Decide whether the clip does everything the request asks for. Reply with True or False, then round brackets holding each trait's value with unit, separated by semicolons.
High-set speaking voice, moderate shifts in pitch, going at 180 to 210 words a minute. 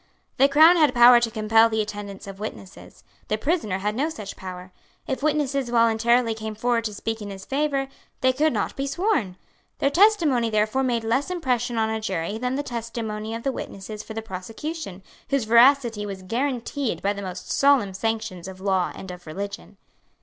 True (225 Hz; 4.6 semitones; 185 wpm)